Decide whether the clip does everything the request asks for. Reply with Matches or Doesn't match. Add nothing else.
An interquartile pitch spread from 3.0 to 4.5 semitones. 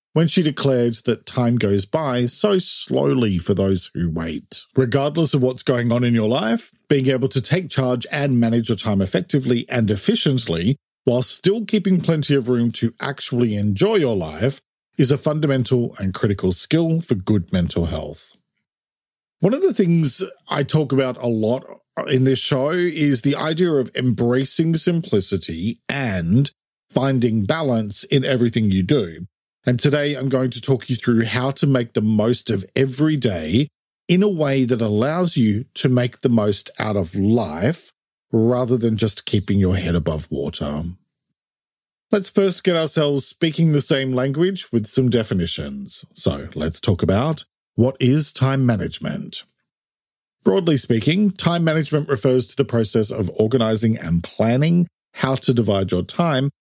Doesn't match